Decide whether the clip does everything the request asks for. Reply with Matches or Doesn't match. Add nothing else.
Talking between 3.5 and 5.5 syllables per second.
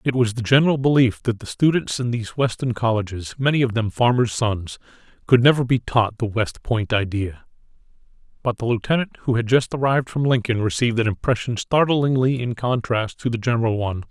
Doesn't match